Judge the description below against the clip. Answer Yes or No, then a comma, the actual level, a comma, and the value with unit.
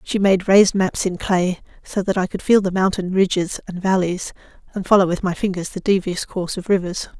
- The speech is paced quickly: Yes, fast, 215 wpm